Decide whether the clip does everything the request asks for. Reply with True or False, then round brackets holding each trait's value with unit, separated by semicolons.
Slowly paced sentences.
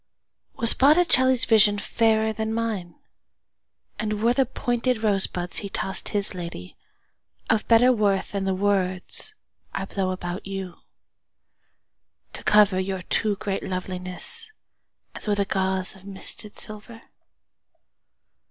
True (95 wpm)